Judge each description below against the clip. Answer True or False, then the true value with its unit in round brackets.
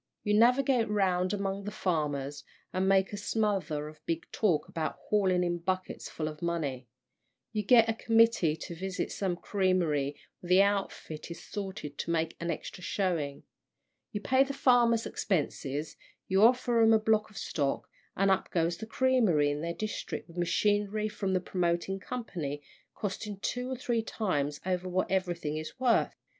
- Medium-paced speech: True (170 wpm)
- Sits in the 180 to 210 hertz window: True (190 Hz)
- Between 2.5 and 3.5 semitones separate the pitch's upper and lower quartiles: False (4.3 semitones)